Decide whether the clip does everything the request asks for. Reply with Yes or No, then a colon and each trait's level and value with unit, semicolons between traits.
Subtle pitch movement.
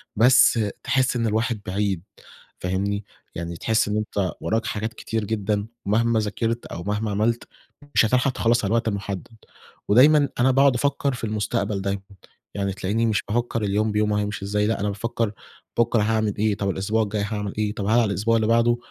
Yes: narrow, 2.3 semitones